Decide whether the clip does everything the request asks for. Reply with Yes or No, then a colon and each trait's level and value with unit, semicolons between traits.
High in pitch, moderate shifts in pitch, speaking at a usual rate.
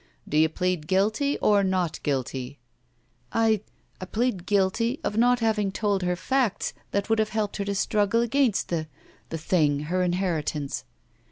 Yes: high, 195 Hz; average, 4.3 semitones; average, 175 wpm